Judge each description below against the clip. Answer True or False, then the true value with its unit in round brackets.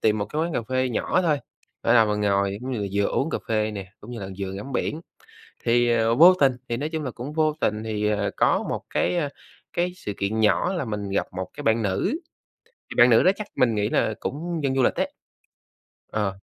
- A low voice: True (115 Hz)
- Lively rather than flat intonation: True (5.8 semitones)